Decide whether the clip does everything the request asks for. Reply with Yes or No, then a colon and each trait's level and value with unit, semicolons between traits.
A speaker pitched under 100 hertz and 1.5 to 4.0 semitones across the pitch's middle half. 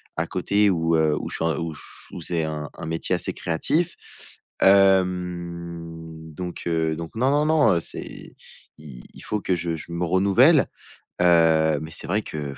Yes: very low, 85 Hz; average, 3.0 semitones